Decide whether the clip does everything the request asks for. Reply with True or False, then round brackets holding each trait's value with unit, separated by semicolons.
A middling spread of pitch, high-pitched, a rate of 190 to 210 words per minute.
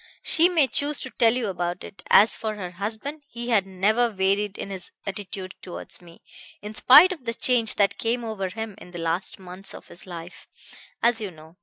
True (4.1 semitones; 205 Hz; 205 wpm)